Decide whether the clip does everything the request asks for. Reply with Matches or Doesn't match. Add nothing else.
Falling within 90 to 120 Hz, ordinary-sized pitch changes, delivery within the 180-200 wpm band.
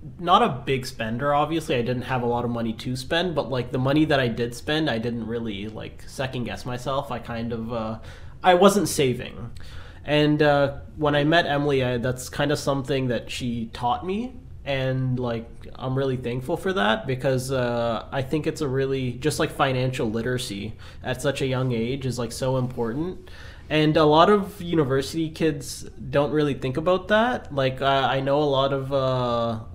Doesn't match